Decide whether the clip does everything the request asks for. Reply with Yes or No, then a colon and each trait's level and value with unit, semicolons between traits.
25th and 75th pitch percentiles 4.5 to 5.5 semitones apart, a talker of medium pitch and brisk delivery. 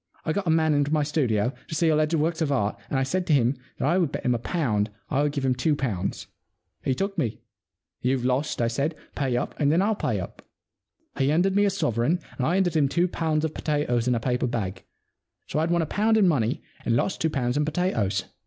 Yes: average, 4.8 semitones; medium, 145 Hz; fast, 245 wpm